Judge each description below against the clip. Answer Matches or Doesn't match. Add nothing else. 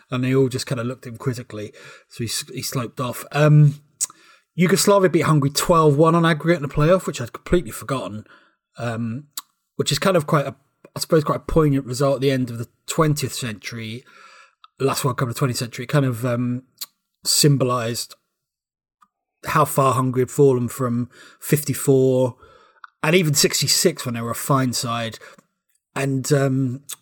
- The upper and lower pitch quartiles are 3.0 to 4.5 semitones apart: Matches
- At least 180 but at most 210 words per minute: Doesn't match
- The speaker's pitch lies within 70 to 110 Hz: Doesn't match